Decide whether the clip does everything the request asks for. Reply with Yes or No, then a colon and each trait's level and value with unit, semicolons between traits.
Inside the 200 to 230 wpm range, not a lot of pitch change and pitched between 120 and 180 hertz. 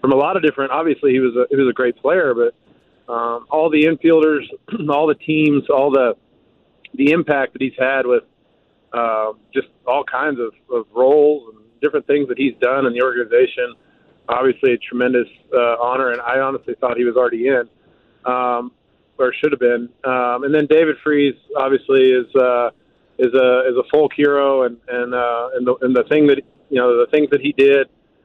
No: fast, 205 wpm; average, 3.4 semitones; low, 130 Hz